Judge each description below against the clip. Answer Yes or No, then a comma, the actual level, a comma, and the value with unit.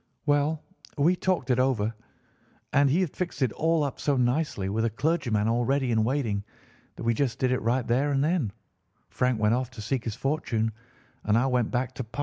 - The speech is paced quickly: Yes, fast, 210 wpm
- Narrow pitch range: No, average, 3.9 semitones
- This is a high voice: No, low, 130 Hz